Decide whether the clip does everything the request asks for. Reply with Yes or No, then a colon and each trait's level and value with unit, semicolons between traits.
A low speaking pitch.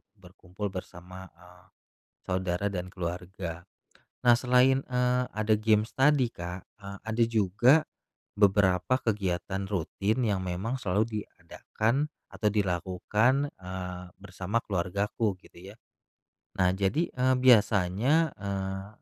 Yes: low, 100 Hz